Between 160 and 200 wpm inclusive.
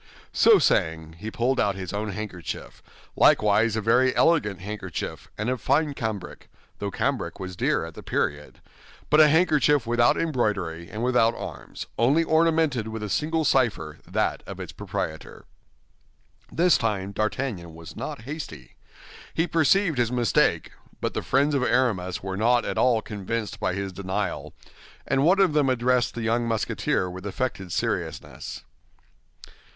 No: average, 150 wpm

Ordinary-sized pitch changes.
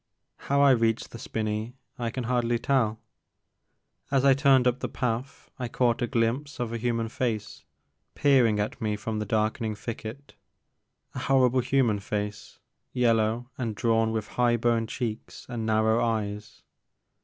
No: narrow, 2.3 semitones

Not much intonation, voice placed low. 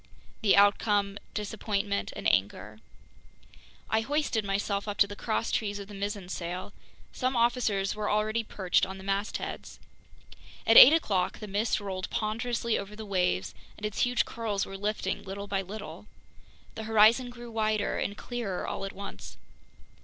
No: narrow, 2.0 semitones; high, 205 Hz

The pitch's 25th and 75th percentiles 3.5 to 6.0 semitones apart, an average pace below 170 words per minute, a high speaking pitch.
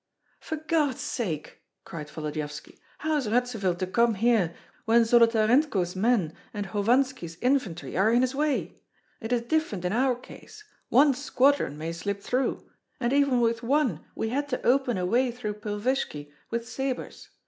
Yes: average, 5.3 semitones; average, 160 wpm; high, 235 Hz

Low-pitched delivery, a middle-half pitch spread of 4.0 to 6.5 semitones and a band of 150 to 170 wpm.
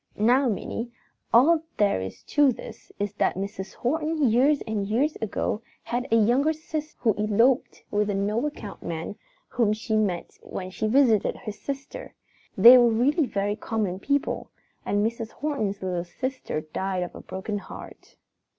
No: high, 220 Hz; average, 4.8 semitones; average, 160 wpm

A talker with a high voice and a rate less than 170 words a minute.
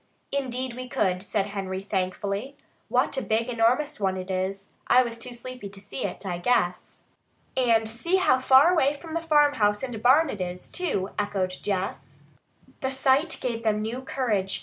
No: high, 230 Hz; average, 175 wpm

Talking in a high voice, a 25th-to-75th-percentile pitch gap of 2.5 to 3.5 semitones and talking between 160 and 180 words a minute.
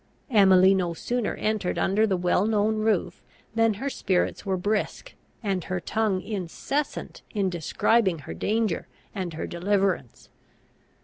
No: high, 195 Hz; average, 3.2 semitones; slow, 135 wpm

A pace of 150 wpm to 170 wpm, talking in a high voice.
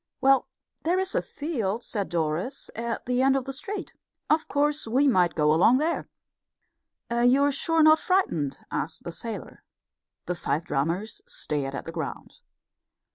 Yes: average, 160 wpm; high, 245 Hz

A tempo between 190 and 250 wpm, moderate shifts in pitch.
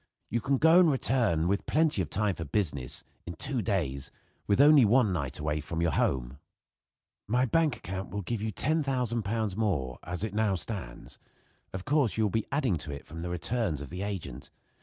No: average, 195 wpm; wide, 6.6 semitones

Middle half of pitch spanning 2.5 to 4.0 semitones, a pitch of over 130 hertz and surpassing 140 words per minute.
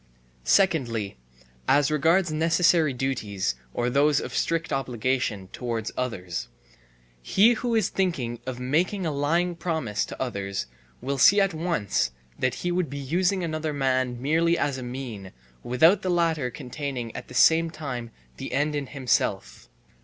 No: average, 5.2 semitones; medium, 140 Hz; average, 150 wpm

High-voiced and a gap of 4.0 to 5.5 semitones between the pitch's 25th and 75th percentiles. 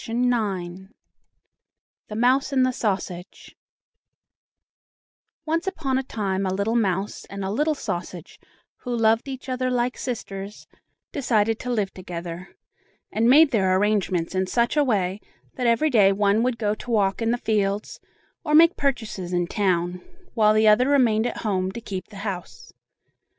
Yes: high, 215 Hz; average, 4.4 semitones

